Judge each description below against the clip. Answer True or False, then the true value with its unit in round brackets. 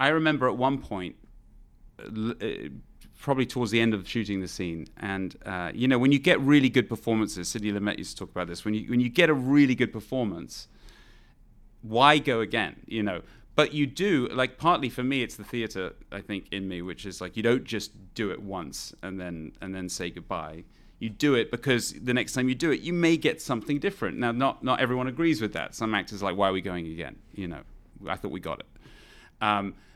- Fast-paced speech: True (225 wpm)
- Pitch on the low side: True (115 Hz)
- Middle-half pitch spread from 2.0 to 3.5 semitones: False (4.9 semitones)